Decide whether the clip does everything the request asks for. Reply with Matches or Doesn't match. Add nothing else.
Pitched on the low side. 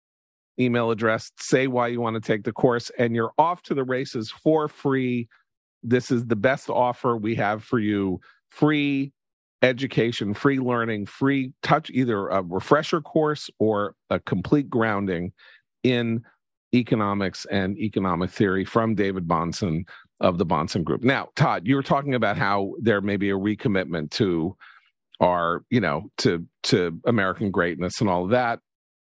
Matches